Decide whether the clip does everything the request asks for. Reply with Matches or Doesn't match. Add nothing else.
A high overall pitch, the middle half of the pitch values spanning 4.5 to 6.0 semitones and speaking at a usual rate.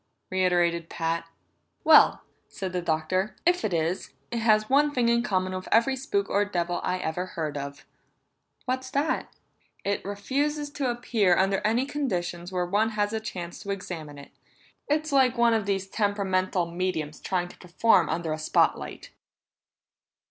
Matches